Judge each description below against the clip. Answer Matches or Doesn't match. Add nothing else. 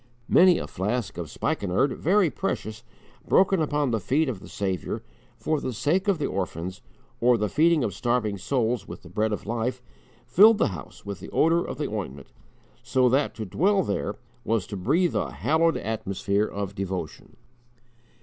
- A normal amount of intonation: Doesn't match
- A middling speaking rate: Matches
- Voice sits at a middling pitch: Doesn't match